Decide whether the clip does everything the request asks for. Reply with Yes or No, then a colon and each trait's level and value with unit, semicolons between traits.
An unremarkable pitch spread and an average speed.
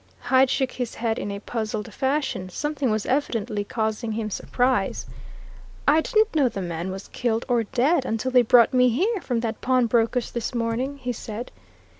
Yes: average, 3.1 semitones; average, 175 wpm